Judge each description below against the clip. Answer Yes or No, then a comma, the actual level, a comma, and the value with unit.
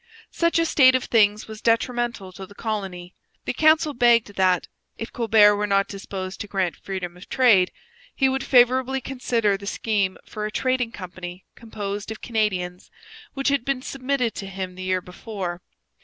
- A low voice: No, high, 210 Hz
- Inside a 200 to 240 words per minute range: No, average, 170 wpm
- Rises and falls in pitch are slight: No, average, 4.7 semitones